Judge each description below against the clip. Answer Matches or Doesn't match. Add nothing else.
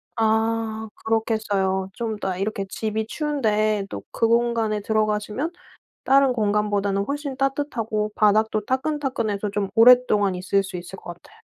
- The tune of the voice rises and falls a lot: Doesn't match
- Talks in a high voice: Matches